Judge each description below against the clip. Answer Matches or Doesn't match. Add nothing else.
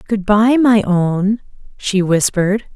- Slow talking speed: Matches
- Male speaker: Doesn't match